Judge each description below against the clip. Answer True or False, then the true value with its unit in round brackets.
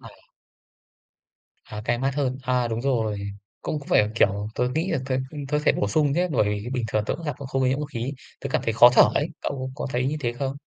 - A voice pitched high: False (130 Hz)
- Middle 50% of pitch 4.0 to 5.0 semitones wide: False (3.5 semitones)